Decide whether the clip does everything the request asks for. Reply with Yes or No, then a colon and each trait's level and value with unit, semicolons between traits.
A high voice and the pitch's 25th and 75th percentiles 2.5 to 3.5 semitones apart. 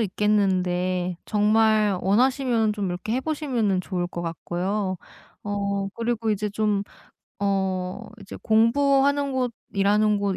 Yes: high, 205 Hz; average, 3.1 semitones